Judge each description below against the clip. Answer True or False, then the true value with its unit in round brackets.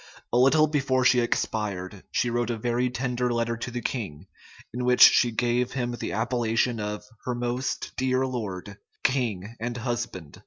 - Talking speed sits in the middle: True (165 wpm)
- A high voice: False (120 Hz)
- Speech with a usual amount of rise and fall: False (2.0 semitones)